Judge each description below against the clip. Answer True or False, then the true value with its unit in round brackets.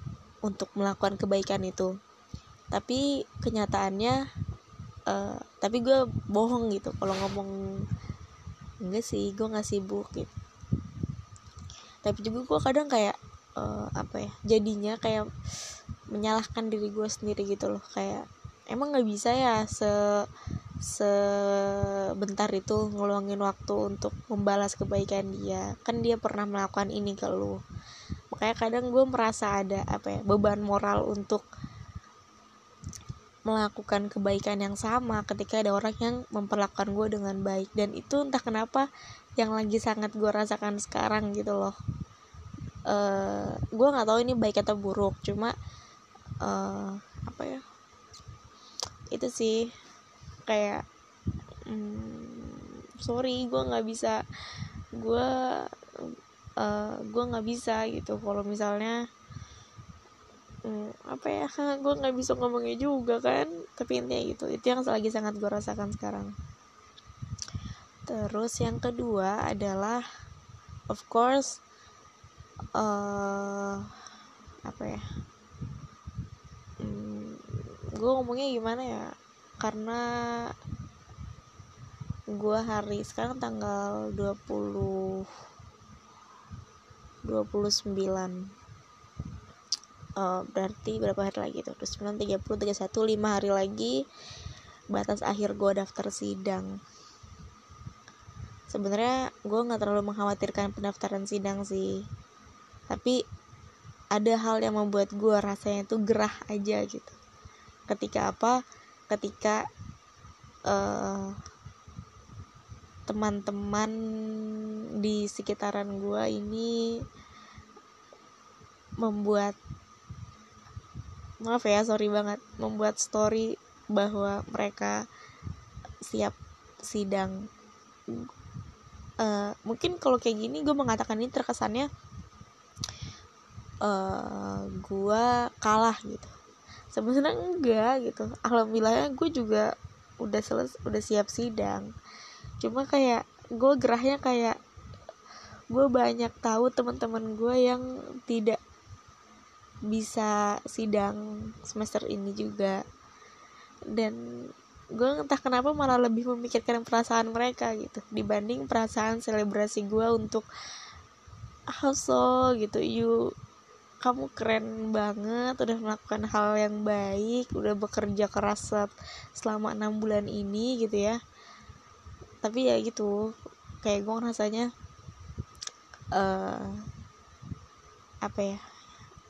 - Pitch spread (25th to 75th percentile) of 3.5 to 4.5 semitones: False (2.7 semitones)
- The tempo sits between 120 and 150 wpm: False (100 wpm)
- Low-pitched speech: False (210 Hz)